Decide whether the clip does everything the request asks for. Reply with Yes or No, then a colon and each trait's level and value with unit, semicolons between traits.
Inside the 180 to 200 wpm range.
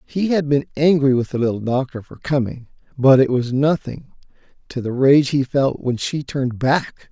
Yes: average, 195 wpm